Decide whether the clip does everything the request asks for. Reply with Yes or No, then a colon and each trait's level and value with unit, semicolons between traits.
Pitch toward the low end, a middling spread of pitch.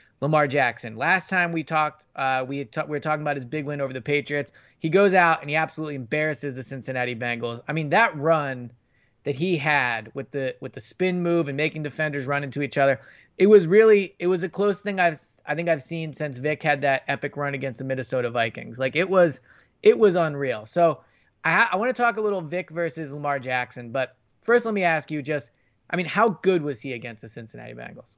No: medium, 150 Hz; average, 4.3 semitones